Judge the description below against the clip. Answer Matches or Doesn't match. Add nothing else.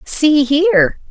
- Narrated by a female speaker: Matches